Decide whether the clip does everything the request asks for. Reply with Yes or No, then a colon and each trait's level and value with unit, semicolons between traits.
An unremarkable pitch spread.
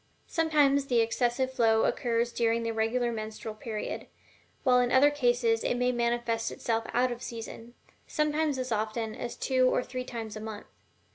No: narrow, 2.1 semitones